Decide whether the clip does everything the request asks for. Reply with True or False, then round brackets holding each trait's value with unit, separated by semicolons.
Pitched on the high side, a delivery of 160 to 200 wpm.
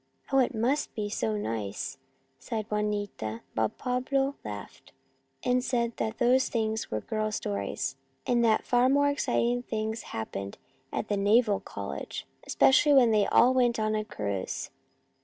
False (220 Hz; 150 wpm)